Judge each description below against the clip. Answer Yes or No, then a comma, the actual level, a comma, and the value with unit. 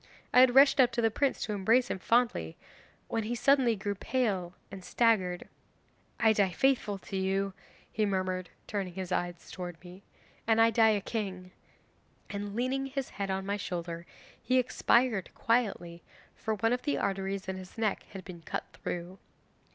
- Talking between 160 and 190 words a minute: Yes, average, 175 wpm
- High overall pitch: Yes, high, 200 Hz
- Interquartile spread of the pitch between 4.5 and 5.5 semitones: No, average, 4.0 semitones